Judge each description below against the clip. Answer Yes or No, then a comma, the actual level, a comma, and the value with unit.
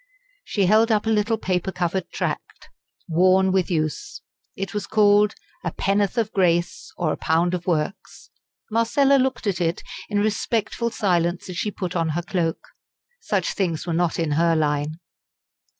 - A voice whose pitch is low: No, medium, 185 Hz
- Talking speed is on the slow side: No, average, 165 wpm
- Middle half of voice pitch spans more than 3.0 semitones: Yes, average, 3.6 semitones